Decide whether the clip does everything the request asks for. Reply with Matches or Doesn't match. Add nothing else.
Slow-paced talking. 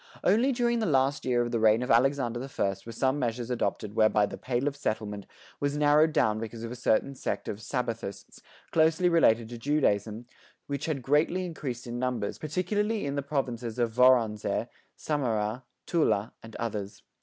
Doesn't match